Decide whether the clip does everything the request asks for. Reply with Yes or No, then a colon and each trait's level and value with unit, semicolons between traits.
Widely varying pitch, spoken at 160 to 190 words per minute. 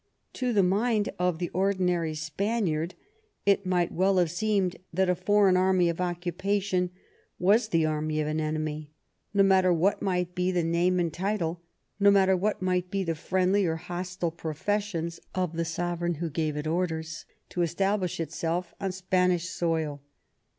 No: narrow, 2.5 semitones; average, 165 wpm